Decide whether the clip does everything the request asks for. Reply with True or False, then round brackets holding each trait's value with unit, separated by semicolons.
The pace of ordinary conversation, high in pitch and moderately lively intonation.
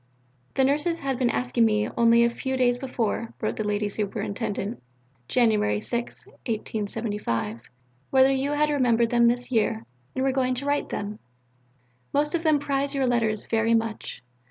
True (165 wpm; 240 Hz; 3.6 semitones)